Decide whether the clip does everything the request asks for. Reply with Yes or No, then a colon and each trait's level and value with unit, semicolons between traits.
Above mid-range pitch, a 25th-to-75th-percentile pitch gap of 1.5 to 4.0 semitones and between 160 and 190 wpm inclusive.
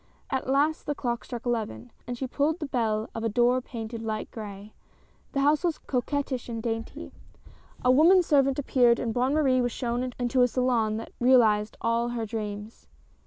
Yes: high, 245 Hz; average, 2.9 semitones; average, 180 wpm